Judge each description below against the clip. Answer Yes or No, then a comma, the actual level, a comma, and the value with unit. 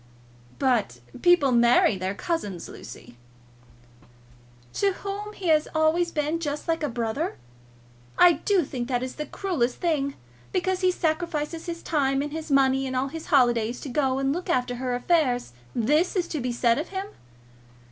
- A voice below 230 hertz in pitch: No, very high, 290 Hz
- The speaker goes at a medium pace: Yes, average, 165 wpm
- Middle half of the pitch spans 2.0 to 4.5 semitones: No, average, 5.3 semitones